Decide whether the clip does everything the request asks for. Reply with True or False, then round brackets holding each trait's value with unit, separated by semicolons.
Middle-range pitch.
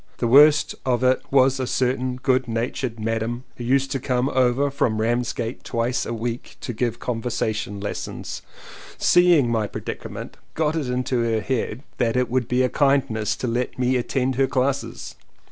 False (125 Hz)